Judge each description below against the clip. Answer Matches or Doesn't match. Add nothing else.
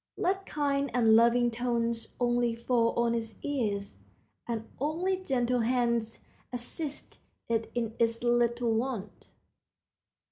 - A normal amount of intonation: Doesn't match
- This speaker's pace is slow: Matches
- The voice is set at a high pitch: Matches